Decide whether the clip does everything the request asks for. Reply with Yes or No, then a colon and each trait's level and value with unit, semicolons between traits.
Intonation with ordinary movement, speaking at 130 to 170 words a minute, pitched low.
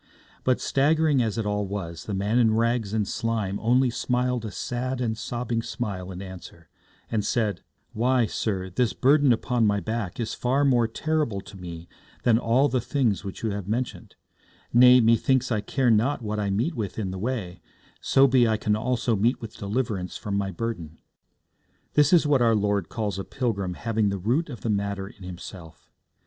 No: average, 3.7 semitones; average, 190 wpm; low, 115 Hz